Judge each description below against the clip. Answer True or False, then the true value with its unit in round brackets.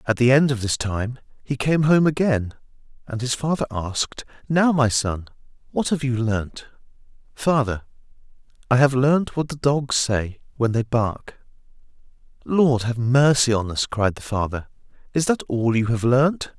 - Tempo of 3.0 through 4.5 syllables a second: True (4.4 syllables/s)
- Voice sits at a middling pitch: False (125 Hz)